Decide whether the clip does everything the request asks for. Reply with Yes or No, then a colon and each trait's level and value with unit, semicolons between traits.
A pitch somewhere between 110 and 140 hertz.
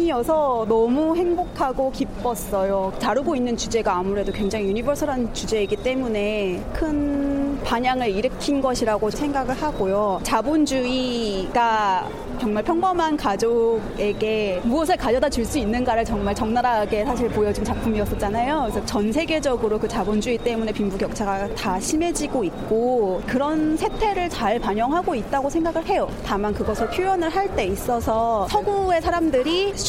No: high, 240 Hz